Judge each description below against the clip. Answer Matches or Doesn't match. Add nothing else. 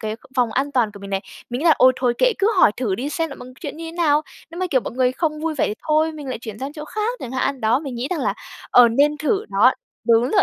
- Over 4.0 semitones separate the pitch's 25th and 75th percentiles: Matches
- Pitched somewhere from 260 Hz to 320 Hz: Matches